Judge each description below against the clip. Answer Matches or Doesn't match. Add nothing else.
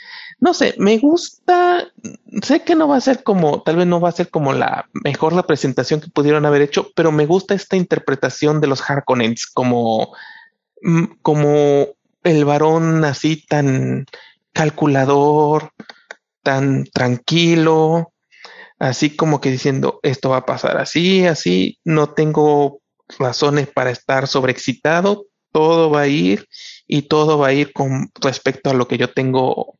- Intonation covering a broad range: Doesn't match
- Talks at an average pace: Matches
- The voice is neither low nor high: Matches